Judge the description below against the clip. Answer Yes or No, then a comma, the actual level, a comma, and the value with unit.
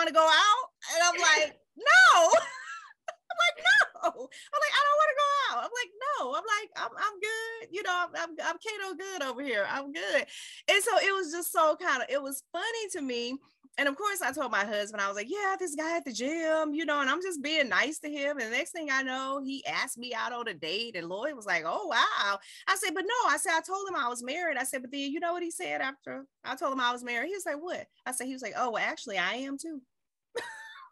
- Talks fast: Yes, fast, 265 wpm